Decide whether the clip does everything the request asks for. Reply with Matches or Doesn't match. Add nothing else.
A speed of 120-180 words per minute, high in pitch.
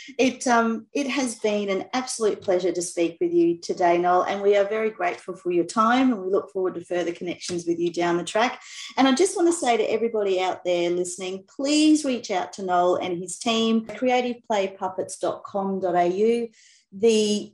Doesn't match